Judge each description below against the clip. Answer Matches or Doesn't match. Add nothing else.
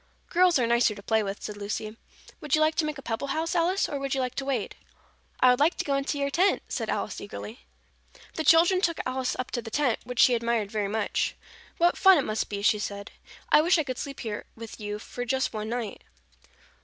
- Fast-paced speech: Matches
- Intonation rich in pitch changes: Matches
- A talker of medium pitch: Doesn't match